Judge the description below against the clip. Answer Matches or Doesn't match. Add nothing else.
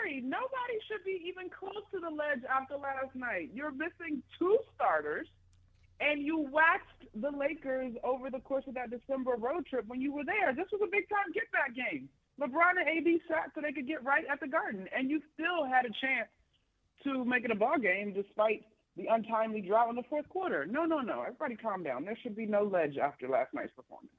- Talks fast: Matches